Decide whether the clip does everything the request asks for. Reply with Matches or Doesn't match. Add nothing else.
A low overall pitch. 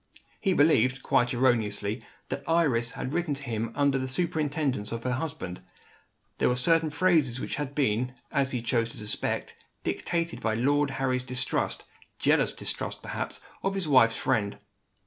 Matches